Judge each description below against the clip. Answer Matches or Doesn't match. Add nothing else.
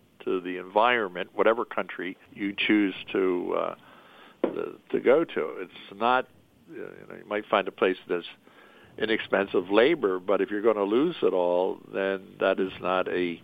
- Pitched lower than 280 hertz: Doesn't match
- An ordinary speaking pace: Matches